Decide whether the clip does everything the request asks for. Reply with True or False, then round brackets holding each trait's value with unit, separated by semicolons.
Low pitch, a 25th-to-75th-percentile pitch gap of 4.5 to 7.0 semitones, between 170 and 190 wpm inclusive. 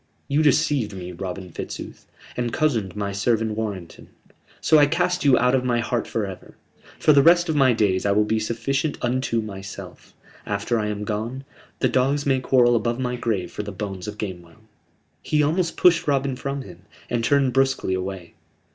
True (120 Hz; 5.1 semitones; 185 wpm)